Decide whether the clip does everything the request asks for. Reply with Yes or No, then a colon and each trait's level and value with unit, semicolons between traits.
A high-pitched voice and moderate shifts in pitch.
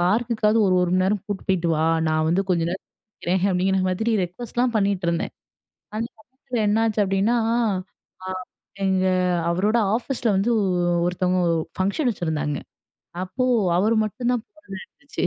Yes: high, 195 Hz; average, 3.9 semitones